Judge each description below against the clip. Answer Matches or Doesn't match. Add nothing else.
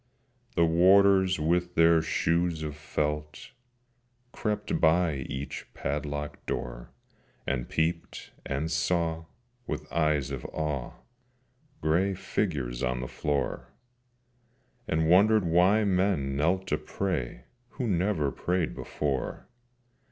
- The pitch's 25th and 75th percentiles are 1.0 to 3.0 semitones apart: Doesn't match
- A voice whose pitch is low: Matches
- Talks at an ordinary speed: Doesn't match